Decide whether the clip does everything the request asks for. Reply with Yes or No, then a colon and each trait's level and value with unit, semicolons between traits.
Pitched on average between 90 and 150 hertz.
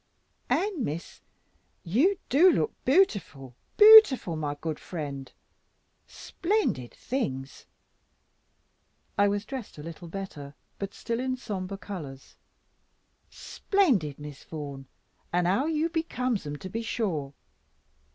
No: high, 195 Hz